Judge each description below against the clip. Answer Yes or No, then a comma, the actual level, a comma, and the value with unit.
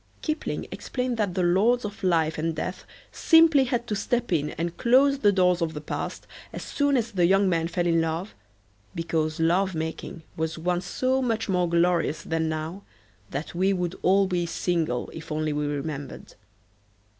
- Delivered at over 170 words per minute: Yes, average, 180 wpm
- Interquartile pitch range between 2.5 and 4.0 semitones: No, average, 4.4 semitones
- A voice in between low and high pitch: Yes, medium, 175 Hz